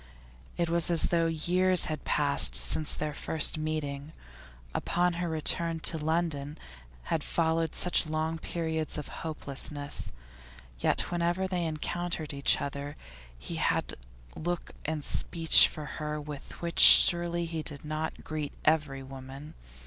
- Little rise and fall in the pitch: Yes, narrow, 2.3 semitones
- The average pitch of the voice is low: No, medium, 155 Hz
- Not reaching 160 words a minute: Yes, slow, 135 wpm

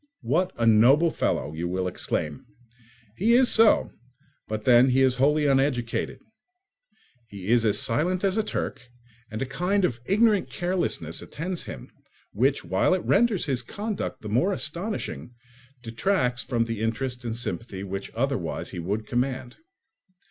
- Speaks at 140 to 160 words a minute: Yes, average, 150 wpm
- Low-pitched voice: Yes, low, 125 Hz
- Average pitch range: No, wide, 8.0 semitones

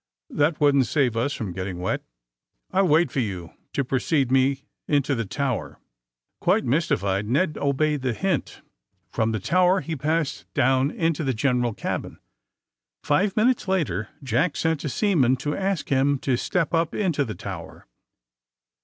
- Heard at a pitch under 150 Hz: Yes, medium, 140 Hz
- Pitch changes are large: No, average, 5.0 semitones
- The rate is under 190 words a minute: Yes, average, 155 wpm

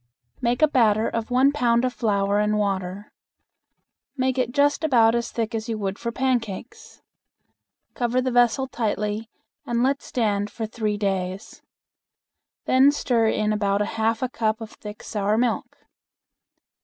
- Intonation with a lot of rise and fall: No, average, 2.9 semitones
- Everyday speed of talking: Yes, average, 155 wpm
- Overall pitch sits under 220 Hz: No, high, 225 Hz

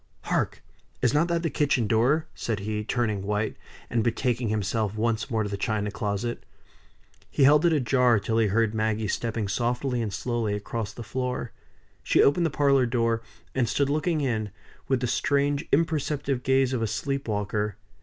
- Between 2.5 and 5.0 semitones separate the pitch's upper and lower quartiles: Yes, average, 4.1 semitones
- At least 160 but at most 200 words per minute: Yes, average, 175 wpm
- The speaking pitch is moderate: No, low, 120 Hz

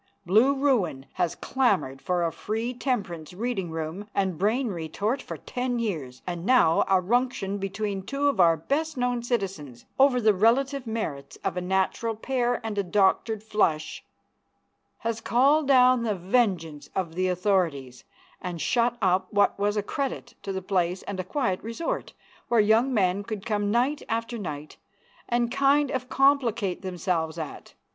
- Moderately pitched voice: No, high, 205 Hz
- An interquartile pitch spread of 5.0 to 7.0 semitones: Yes, average, 5.3 semitones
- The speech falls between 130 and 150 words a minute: No, average, 160 wpm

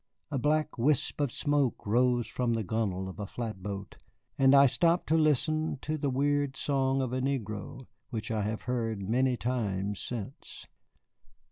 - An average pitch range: Yes, average, 4.4 semitones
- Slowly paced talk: No, average, 160 wpm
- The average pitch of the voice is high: No, low, 125 Hz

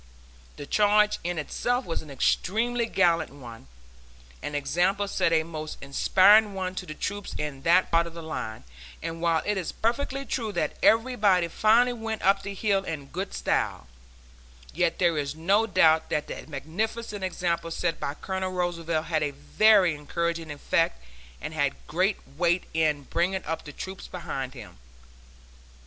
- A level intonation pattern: No, average, 4.4 semitones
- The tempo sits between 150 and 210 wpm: Yes, average, 165 wpm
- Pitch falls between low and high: Yes, medium, 175 Hz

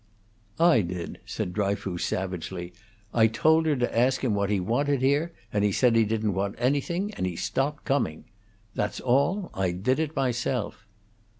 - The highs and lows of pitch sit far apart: Yes, wide, 6.1 semitones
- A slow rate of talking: No, average, 170 wpm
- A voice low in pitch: Yes, low, 115 Hz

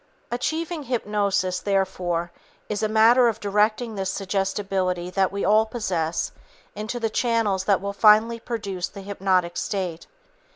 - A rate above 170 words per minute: No, slow, 135 wpm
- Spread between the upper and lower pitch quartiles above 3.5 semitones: No, average, 2.9 semitones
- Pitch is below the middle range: No, high, 200 Hz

